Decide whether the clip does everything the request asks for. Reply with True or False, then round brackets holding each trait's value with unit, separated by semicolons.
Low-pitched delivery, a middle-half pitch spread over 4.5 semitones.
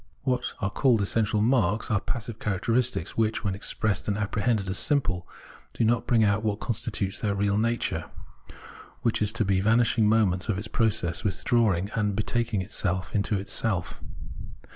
False (105 Hz; 2.5 semitones)